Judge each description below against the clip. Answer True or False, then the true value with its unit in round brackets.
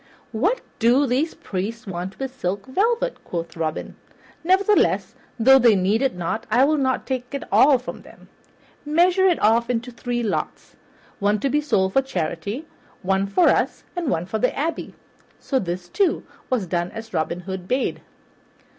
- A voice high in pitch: True (235 Hz)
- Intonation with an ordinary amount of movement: False (6.5 semitones)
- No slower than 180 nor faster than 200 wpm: False (165 wpm)